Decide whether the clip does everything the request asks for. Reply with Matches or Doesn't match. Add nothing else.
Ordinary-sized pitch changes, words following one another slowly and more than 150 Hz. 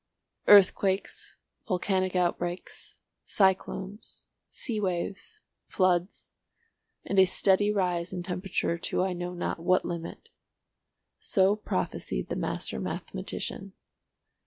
Doesn't match